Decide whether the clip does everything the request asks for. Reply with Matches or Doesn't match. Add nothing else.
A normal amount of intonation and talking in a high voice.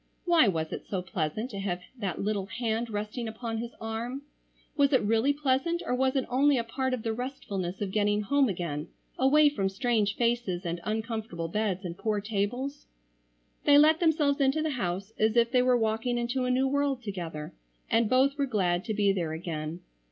Matches